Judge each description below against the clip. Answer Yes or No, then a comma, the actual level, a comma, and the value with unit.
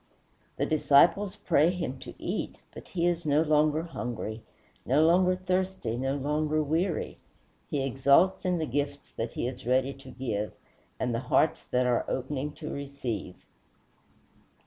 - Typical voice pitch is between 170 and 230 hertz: No, medium, 145 Hz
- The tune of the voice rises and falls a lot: No, average, 4.3 semitones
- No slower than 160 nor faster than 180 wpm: No, average, 150 wpm